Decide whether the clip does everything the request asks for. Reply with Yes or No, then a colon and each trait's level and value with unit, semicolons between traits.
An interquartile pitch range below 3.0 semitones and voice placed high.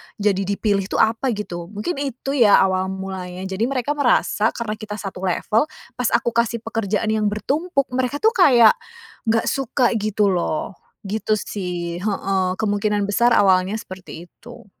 No: average, 3.6 semitones; high, 210 Hz